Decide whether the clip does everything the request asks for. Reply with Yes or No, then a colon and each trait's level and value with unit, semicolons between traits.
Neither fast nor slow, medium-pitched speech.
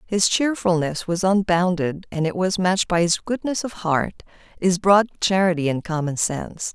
Yes: average, 170 wpm; medium, 180 Hz